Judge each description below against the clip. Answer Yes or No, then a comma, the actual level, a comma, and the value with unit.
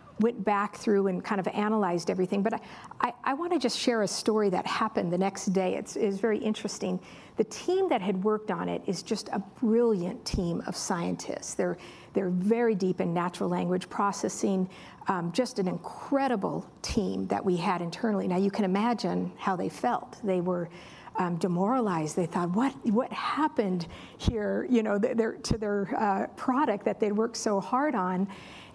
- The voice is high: Yes, high, 205 Hz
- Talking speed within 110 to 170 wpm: No, average, 185 wpm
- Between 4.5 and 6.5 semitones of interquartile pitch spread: No, average, 3.7 semitones